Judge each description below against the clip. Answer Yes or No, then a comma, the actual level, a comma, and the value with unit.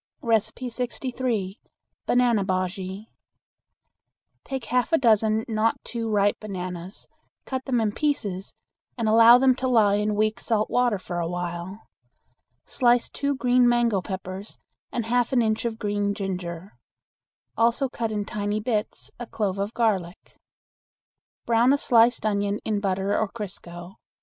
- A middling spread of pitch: Yes, average, 3.5 semitones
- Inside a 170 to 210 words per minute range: No, average, 140 wpm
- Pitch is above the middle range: Yes, high, 215 Hz